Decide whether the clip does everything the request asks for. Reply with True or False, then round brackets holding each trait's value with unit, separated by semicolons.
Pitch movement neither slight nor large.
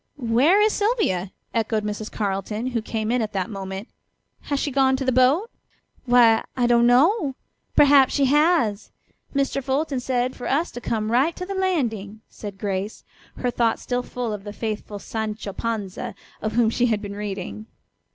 True (4.3 semitones)